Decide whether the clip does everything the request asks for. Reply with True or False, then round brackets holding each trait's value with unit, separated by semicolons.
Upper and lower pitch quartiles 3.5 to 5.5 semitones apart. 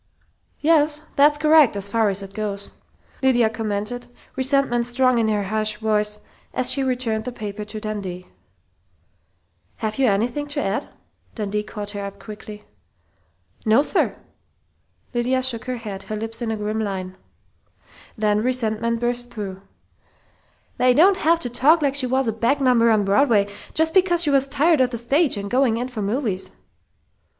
True (3.9 semitones)